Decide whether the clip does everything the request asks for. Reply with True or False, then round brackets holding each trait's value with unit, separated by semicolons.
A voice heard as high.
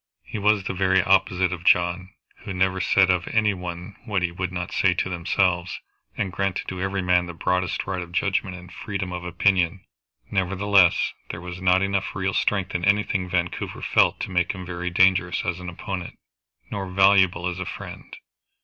False (90 Hz)